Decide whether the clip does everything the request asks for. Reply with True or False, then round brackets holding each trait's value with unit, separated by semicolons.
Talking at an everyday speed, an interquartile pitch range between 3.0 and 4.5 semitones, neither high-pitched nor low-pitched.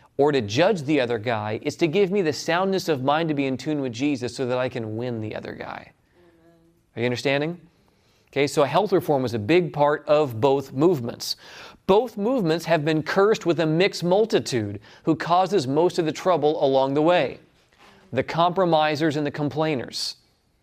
True (190 wpm; 4.2 semitones; 155 Hz)